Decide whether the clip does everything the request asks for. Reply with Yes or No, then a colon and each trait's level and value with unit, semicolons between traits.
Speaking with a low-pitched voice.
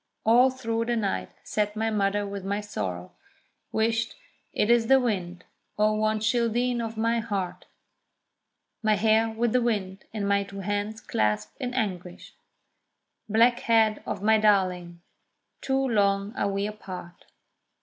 No: high, 215 Hz